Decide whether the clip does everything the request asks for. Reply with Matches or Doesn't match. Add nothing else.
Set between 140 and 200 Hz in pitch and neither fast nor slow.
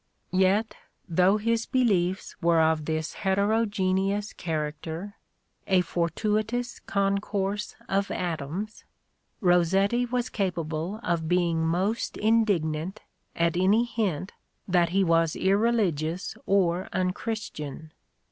Doesn't match